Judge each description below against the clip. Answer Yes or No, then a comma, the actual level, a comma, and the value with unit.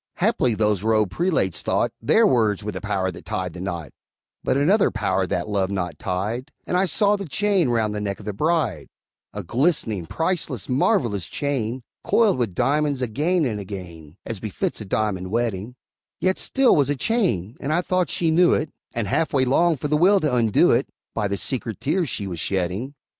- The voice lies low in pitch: Yes, low, 115 Hz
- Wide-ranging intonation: Yes, wide, 7.7 semitones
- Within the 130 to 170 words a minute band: No, average, 195 wpm